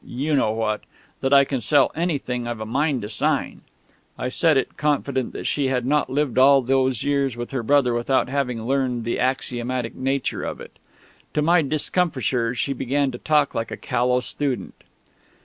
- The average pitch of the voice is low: Yes, low, 130 Hz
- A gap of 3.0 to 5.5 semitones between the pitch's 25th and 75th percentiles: No, narrow, 2.6 semitones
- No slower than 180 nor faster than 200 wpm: Yes, average, 185 wpm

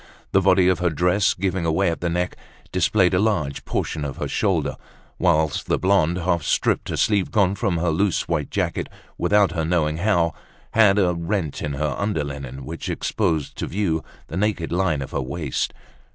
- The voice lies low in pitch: Yes, very low, 85 Hz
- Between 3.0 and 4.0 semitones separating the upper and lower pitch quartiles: Yes, average, 3.6 semitones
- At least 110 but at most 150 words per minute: No, average, 185 wpm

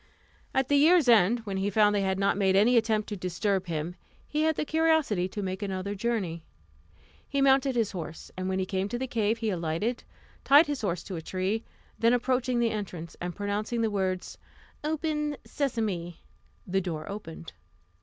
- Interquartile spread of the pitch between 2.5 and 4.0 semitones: No, average, 4.8 semitones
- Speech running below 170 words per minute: No, average, 185 wpm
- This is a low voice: No, high, 205 Hz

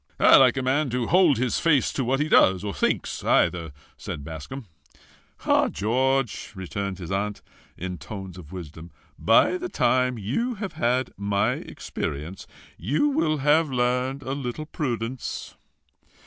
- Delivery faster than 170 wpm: No, average, 150 wpm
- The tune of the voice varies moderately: No, wide, 6.0 semitones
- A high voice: No, low, 125 Hz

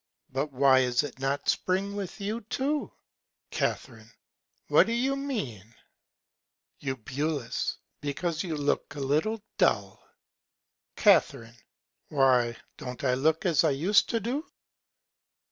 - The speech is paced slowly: Yes, slow, 120 wpm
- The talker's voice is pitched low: No, medium, 150 Hz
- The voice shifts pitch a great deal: Yes, wide, 7.4 semitones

